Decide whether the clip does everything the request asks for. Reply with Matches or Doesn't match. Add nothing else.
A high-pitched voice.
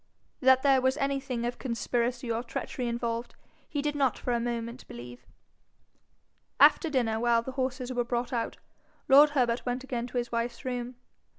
Matches